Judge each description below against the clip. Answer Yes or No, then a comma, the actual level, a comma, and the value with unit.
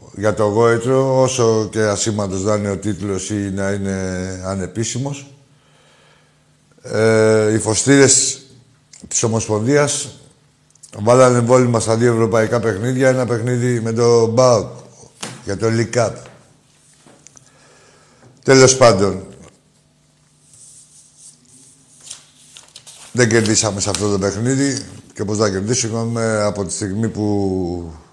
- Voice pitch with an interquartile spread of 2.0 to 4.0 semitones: Yes, average, 3.7 semitones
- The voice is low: Yes, low, 115 Hz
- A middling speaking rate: No, slow, 105 wpm